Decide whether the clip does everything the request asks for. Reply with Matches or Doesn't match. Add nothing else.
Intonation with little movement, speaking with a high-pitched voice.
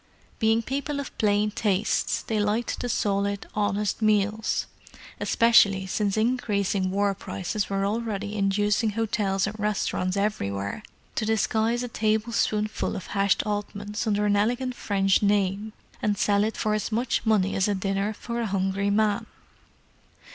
Matches